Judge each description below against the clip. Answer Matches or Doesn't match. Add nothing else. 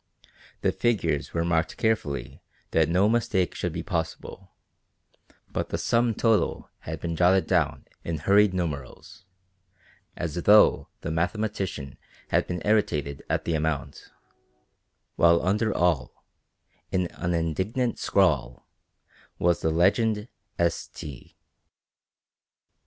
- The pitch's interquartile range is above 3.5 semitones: Matches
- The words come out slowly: Matches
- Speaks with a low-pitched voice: Matches